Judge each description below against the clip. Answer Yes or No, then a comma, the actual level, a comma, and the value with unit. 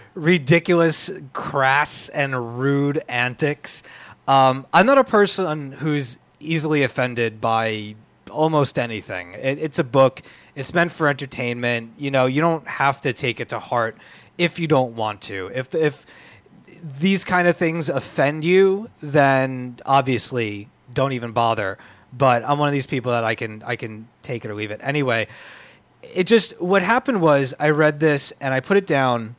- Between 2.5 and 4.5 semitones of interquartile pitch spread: No, average, 4.9 semitones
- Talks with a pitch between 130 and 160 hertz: Yes, medium, 140 Hz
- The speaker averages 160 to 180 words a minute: Yes, average, 165 wpm